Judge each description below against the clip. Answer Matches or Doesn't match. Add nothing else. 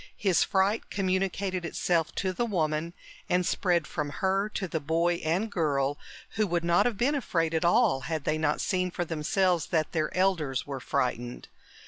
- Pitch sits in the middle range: Matches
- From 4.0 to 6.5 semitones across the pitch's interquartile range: Doesn't match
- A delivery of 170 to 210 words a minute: Matches